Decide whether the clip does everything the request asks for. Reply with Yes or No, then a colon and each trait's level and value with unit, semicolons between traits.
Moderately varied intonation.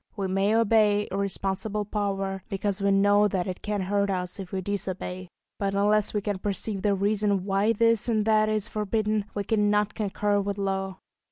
No: narrow, 1.4 semitones